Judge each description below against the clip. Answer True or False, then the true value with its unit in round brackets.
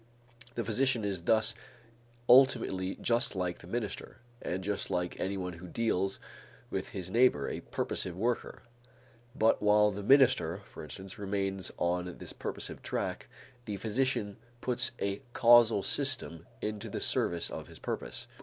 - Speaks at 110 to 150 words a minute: True (145 wpm)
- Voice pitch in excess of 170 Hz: False (100 Hz)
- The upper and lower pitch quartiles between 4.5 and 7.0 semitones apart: False (4.1 semitones)